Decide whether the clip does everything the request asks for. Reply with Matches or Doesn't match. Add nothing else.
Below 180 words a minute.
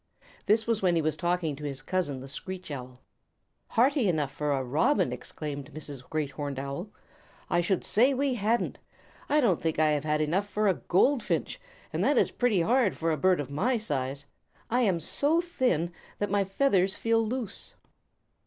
Doesn't match